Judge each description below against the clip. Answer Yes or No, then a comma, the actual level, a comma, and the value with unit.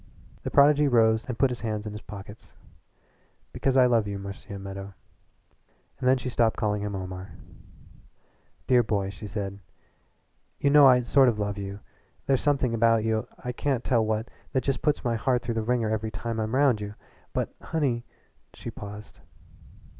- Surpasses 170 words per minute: Yes, average, 180 wpm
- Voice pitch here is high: No, low, 115 Hz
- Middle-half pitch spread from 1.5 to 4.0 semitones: Yes, average, 3.5 semitones